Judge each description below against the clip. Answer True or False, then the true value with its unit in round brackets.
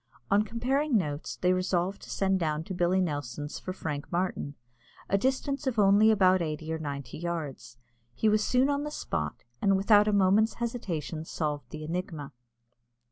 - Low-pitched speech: False (185 Hz)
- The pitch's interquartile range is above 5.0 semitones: True (5.5 semitones)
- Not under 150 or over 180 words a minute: True (170 wpm)